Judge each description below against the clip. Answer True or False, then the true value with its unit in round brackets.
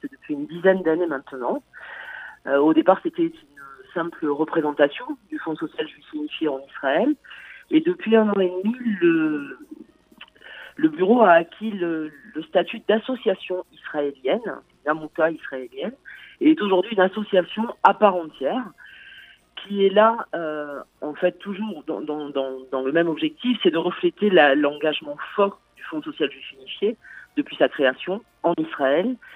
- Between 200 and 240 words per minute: False (150 wpm)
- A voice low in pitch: False (190 Hz)